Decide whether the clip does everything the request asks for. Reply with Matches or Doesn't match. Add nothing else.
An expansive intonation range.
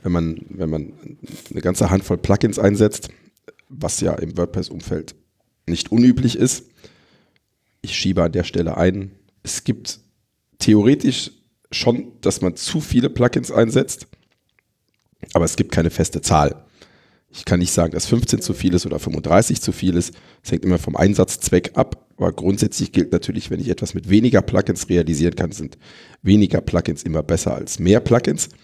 Doesn't match